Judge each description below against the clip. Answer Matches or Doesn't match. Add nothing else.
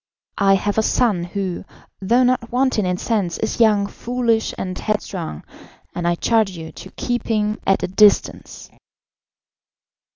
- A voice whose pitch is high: Matches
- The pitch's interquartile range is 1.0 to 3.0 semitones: Doesn't match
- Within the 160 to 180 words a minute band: Doesn't match